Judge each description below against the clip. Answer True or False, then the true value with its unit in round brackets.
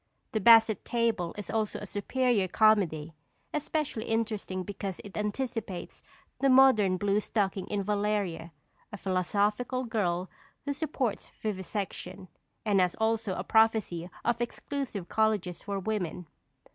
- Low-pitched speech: False (210 Hz)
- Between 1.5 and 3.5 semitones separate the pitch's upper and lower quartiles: True (3.2 semitones)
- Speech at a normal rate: False (125 wpm)